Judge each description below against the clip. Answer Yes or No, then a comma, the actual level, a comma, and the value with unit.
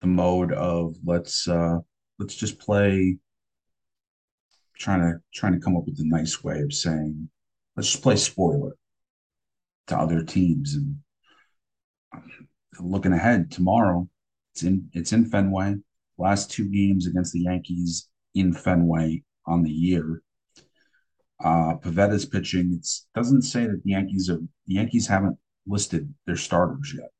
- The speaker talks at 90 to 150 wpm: Yes, average, 140 wpm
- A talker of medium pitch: No, very low, 90 Hz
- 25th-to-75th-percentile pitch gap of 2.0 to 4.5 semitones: Yes, average, 2.9 semitones